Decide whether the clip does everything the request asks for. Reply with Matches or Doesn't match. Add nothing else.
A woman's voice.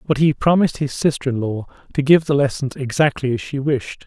Doesn't match